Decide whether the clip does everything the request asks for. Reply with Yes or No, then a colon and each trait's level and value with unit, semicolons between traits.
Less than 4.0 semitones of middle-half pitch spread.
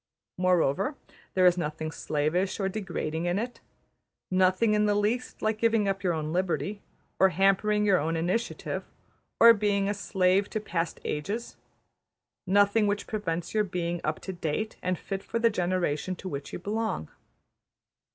Yes: average, 3.3 semitones